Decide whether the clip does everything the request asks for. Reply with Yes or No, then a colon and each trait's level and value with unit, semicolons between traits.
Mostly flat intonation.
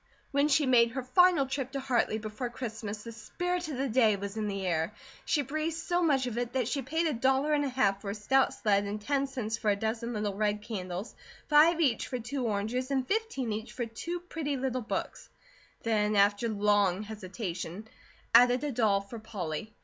No: average, 4.5 semitones